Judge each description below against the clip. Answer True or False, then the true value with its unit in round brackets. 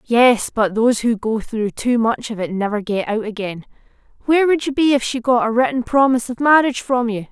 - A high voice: True (235 Hz)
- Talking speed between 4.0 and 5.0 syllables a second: False (5.6 syllables/s)